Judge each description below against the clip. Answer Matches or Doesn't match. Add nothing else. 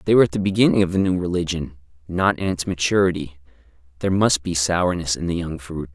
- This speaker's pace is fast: Matches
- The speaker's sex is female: Doesn't match